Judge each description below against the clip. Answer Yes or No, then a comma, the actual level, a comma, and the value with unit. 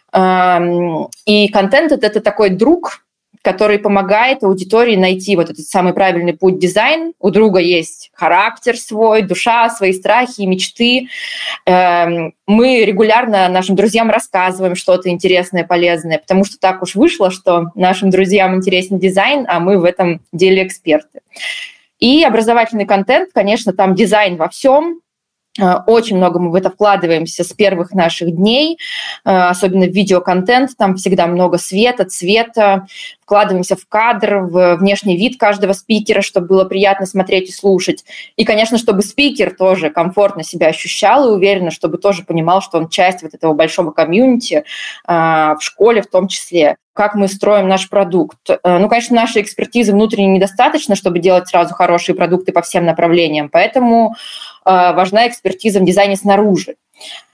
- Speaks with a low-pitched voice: No, high, 195 Hz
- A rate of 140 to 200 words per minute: Yes, average, 145 wpm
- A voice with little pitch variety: No, average, 3.3 semitones